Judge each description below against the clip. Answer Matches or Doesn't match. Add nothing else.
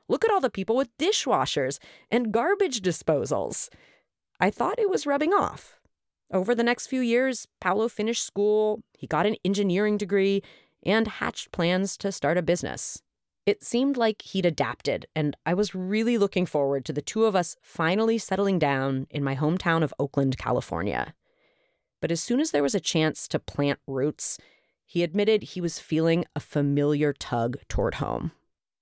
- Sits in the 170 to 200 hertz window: Matches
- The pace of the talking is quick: Doesn't match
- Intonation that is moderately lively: Doesn't match